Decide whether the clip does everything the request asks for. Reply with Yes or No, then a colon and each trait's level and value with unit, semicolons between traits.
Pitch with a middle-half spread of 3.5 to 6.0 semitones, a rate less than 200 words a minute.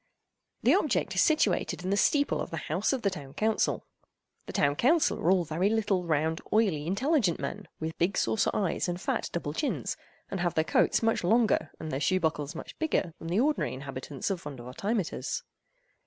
Yes: wide, 5.5 semitones; average, 190 wpm